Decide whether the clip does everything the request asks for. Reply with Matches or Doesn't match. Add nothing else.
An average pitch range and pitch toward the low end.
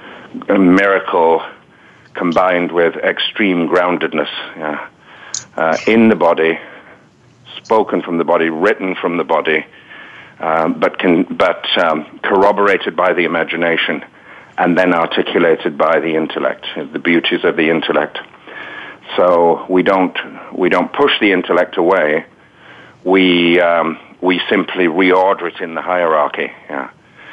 Doesn't match